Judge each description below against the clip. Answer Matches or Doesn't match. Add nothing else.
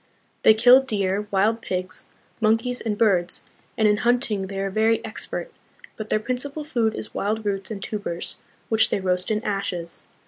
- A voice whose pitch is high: Matches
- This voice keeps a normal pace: Matches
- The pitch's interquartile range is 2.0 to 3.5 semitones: Matches